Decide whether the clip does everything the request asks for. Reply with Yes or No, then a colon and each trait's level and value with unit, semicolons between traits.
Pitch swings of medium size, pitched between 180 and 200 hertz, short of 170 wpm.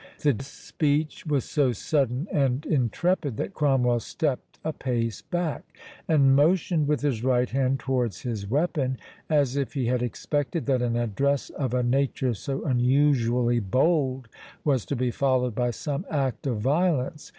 No: average, 3.1 semitones; low, 135 Hz; average, 155 wpm